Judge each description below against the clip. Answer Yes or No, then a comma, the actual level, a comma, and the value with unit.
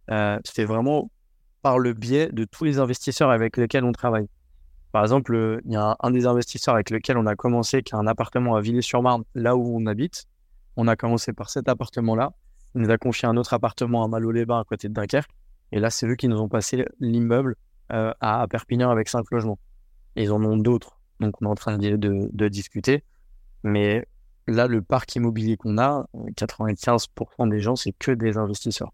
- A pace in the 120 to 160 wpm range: No, average, 210 wpm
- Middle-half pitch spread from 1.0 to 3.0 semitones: Yes, narrow, 2.4 semitones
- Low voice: Yes, low, 115 Hz